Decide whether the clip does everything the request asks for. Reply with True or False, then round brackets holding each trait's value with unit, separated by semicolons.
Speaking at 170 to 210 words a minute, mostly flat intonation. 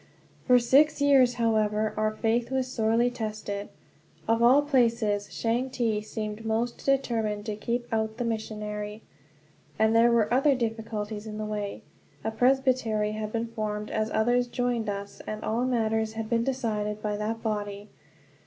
False (155 wpm; 2.2 semitones)